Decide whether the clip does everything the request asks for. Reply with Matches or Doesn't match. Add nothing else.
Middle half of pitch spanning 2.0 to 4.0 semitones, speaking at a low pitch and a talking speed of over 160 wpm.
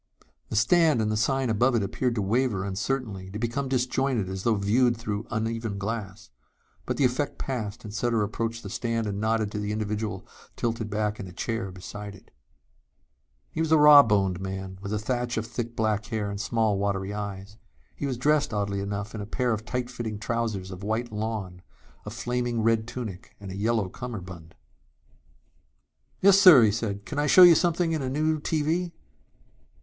Matches